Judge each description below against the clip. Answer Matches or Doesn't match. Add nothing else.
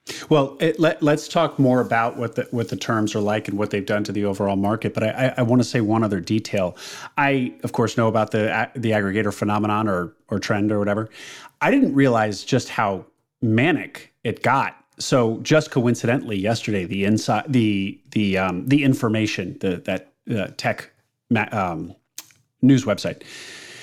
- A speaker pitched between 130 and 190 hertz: Doesn't match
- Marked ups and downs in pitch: Doesn't match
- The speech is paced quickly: Doesn't match